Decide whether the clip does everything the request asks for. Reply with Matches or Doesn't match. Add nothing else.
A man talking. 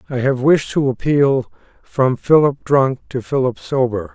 Matches